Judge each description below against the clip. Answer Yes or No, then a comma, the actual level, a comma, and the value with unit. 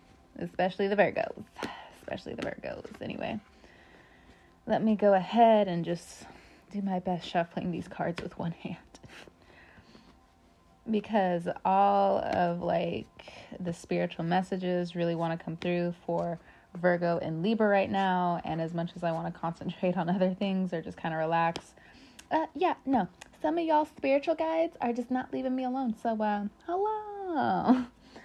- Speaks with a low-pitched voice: No, medium, 185 Hz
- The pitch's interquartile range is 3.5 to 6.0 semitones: Yes, average, 4.8 semitones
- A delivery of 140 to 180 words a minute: Yes, average, 155 wpm